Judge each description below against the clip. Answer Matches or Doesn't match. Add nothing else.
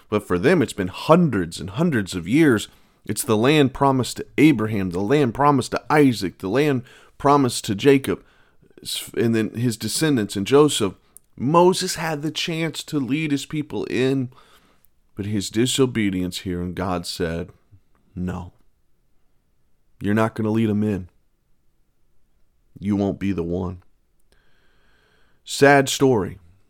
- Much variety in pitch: Matches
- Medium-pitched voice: Doesn't match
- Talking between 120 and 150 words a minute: Matches